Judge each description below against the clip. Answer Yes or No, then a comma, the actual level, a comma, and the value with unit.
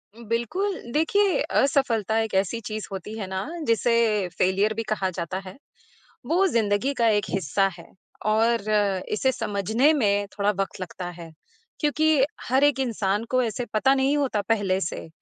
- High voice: Yes, high, 220 Hz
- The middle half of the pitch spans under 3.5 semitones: No, average, 4.9 semitones